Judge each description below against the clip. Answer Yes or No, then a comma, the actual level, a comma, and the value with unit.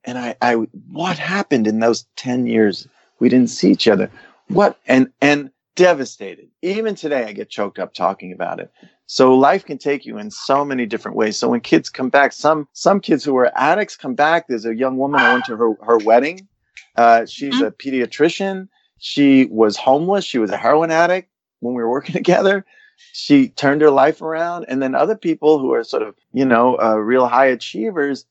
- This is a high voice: No, medium, 140 Hz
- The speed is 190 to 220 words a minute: Yes, fast, 205 wpm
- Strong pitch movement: Yes, wide, 6.6 semitones